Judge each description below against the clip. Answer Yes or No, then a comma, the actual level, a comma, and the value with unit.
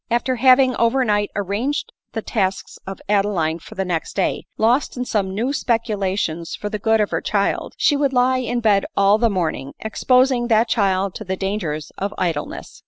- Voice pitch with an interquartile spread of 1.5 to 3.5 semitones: No, average, 4.0 semitones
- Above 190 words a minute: Yes, average, 200 wpm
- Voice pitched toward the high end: Yes, high, 210 Hz